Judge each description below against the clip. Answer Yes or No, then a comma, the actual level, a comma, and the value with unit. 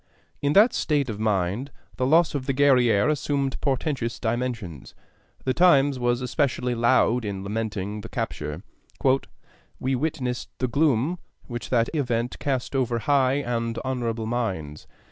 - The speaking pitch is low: Yes, low, 125 Hz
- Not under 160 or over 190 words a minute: No, average, 140 wpm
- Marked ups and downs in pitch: No, average, 3.4 semitones